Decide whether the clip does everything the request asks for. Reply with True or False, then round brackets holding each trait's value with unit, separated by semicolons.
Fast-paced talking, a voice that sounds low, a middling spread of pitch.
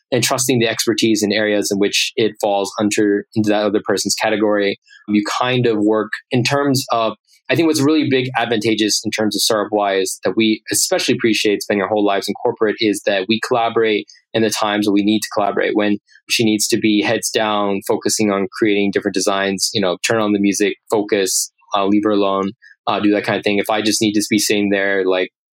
False (220 wpm; 105 Hz; 1.8 semitones)